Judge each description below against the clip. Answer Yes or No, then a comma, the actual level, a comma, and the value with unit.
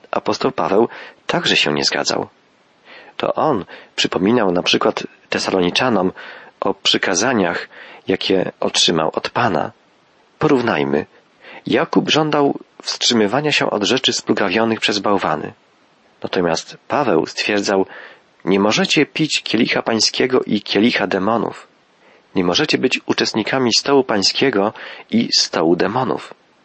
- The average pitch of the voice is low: Yes, low, 120 Hz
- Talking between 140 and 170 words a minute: No, slow, 110 wpm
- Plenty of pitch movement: Yes, wide, 6.3 semitones